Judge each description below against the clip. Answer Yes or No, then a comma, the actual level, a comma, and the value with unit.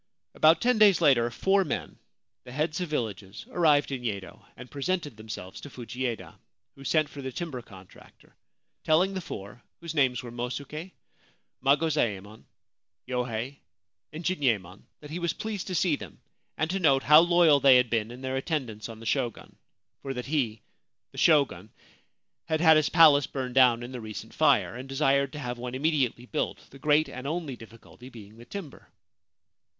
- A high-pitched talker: No, low, 135 Hz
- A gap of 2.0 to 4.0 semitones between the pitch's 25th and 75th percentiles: No, average, 4.7 semitones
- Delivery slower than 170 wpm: No, average, 175 wpm